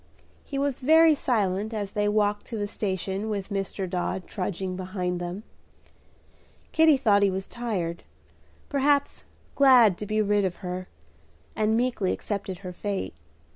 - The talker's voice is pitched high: Yes, high, 205 Hz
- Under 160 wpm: Yes, average, 145 wpm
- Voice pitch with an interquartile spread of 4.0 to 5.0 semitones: No, average, 3.6 semitones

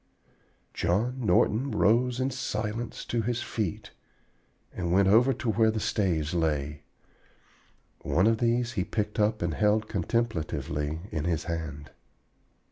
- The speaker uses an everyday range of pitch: No, wide, 5.7 semitones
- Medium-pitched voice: No, low, 105 Hz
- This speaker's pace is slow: Yes, slow, 130 wpm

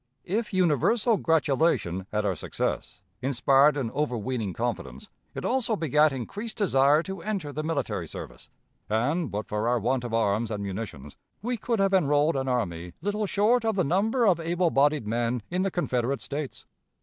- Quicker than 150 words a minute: Yes, average, 170 wpm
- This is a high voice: No, medium, 145 Hz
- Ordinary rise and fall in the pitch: No, wide, 8.2 semitones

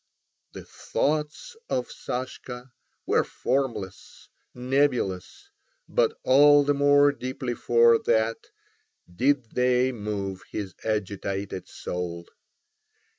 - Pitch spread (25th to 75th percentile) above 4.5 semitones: Yes, average, 5.2 semitones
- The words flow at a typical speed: No, slow, 90 wpm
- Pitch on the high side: No, low, 125 Hz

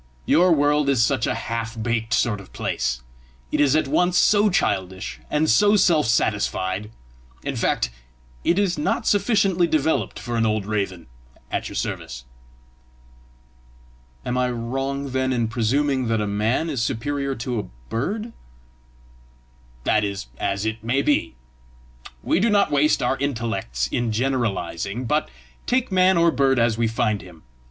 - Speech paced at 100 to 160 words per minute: Yes, average, 155 wpm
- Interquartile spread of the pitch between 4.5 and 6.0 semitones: Yes, wide, 5.6 semitones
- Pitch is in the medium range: No, low, 125 Hz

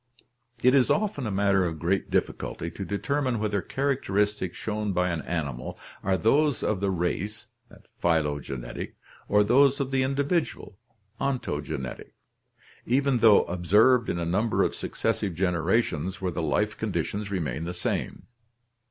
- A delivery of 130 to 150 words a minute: Yes, average, 145 wpm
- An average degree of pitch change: No, wide, 6.3 semitones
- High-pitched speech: No, low, 100 Hz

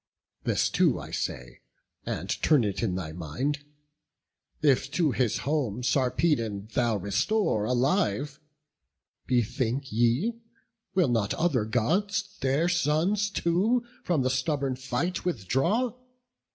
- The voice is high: No, low, 135 Hz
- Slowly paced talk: Yes, slow, 115 wpm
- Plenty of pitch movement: Yes, wide, 7.0 semitones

